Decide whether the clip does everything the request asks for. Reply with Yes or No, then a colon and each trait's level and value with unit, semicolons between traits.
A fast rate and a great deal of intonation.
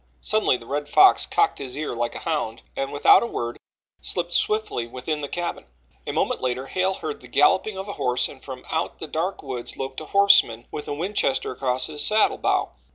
Yes: fast, 210 wpm; wide, 6.8 semitones